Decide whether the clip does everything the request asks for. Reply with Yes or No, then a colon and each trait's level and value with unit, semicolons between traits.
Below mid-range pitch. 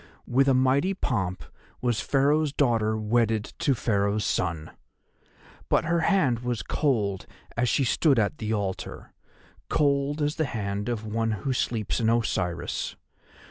Yes: low, 120 Hz